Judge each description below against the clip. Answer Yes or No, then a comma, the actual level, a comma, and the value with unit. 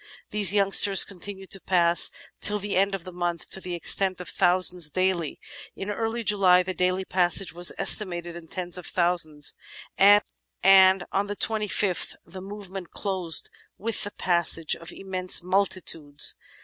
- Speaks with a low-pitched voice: No, medium, 185 Hz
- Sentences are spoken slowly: No, average, 155 wpm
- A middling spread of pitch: No, narrow, 2.1 semitones